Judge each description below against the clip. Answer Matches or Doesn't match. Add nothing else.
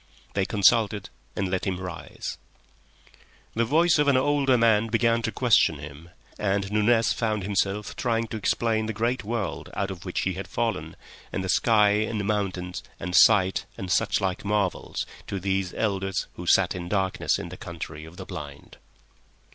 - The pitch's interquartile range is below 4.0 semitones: Matches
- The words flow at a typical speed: Matches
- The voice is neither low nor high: Doesn't match